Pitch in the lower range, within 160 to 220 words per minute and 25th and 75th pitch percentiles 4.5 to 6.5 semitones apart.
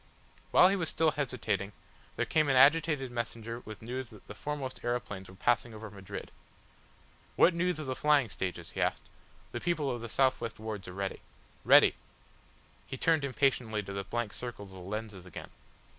Yes: low, 120 Hz; average, 185 wpm; average, 5.1 semitones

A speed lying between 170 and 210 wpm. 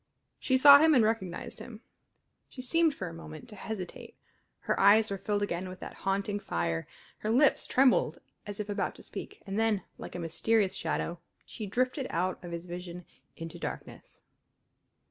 Yes: average, 175 wpm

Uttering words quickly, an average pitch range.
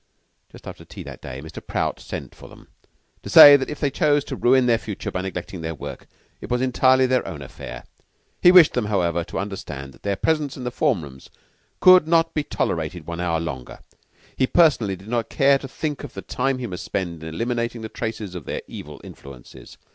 No: fast, 215 wpm; wide, 8.0 semitones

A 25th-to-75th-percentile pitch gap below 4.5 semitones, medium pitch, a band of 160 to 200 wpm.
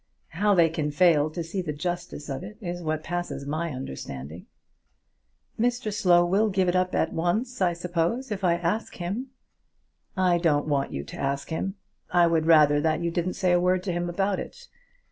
Yes: average, 2.9 semitones; medium, 175 Hz; average, 190 wpm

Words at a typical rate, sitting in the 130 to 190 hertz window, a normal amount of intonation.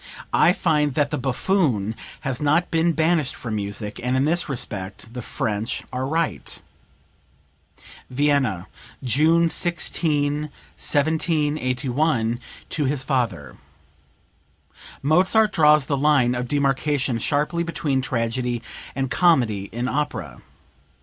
No: slow, 110 wpm; medium, 140 Hz; average, 4.2 semitones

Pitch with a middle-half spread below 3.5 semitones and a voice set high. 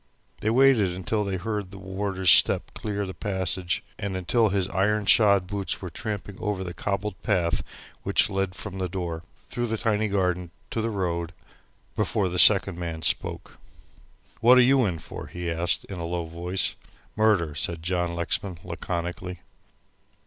No: average, 2.8 semitones; very low, 95 Hz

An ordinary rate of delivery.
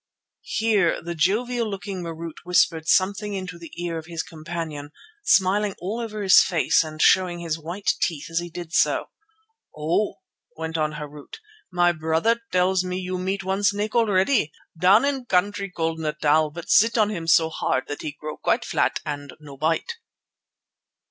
Yes: average, 170 wpm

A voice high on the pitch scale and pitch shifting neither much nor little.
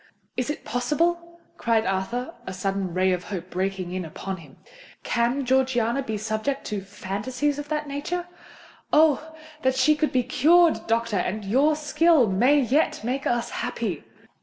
No: high, 245 Hz; wide, 6.9 semitones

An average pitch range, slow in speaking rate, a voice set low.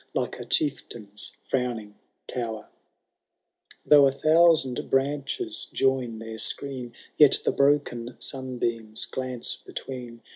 Yes: average, 3.0 semitones; slow, 105 wpm; low, 130 Hz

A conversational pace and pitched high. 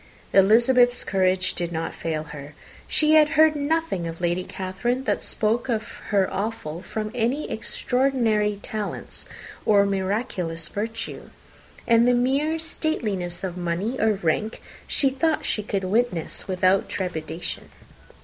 No: slow, 130 wpm; high, 210 Hz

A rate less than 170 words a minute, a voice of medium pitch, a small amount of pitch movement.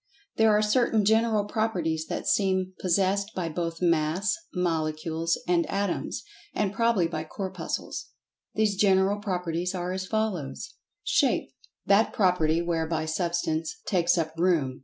No: slow, 135 wpm; medium, 180 Hz; average, 3.7 semitones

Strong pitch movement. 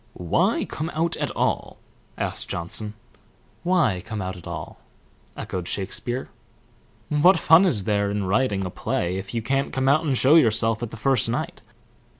Yes: wide, 6.3 semitones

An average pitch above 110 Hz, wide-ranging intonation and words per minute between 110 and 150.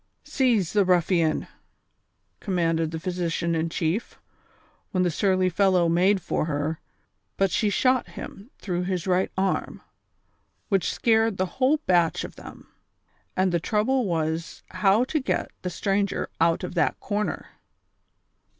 No: medium, 185 Hz; average, 3.4 semitones; average, 145 wpm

